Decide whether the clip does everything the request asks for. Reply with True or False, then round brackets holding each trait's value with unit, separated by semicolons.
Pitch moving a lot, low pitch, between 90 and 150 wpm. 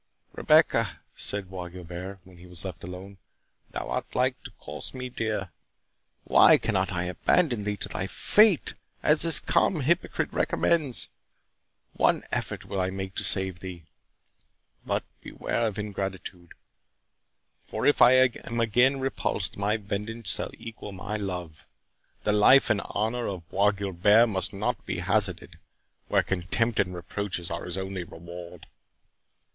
False (4.1 semitones; 100 Hz; 140 wpm)